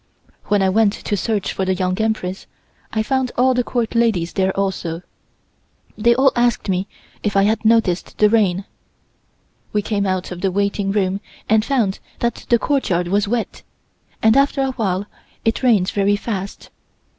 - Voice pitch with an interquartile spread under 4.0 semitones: Yes, average, 3.3 semitones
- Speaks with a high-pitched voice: Yes, high, 205 Hz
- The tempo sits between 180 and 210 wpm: No, average, 170 wpm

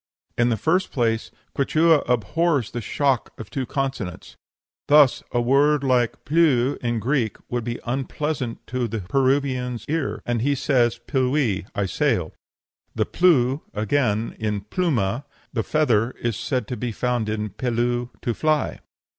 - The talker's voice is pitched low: Yes, low, 125 Hz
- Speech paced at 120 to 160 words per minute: Yes, average, 145 wpm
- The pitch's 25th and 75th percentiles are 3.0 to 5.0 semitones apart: Yes, average, 3.7 semitones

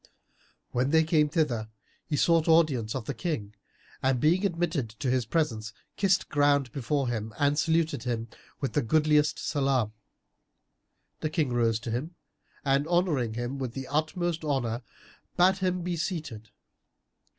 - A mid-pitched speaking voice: Yes, medium, 145 Hz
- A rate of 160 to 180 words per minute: No, average, 150 wpm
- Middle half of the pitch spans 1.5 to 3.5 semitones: No, average, 5.0 semitones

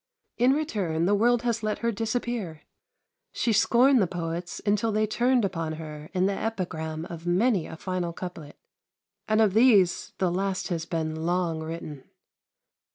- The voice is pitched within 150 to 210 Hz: Yes, medium, 185 Hz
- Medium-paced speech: Yes, average, 160 wpm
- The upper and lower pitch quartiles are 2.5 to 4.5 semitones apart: No, average, 5.2 semitones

